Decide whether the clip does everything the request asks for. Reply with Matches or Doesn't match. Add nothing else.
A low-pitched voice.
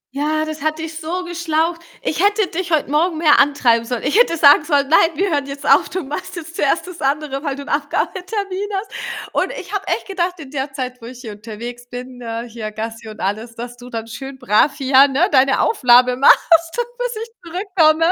Doesn't match